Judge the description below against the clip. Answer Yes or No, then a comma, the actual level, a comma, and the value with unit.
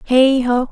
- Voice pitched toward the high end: Yes, very high, 255 Hz